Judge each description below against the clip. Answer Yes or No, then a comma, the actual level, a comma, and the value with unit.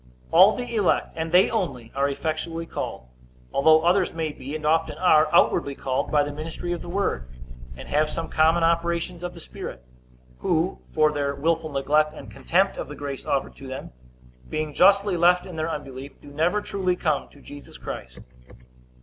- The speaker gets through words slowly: No, average, 185 wpm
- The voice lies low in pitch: No, medium, 160 Hz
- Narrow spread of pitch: No, average, 3.3 semitones